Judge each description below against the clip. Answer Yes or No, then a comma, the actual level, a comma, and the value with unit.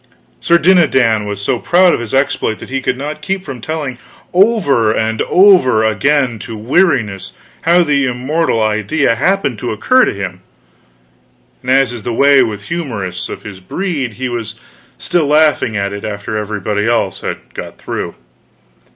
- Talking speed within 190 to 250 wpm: No, average, 165 wpm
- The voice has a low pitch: Yes, low, 125 Hz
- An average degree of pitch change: No, wide, 6.1 semitones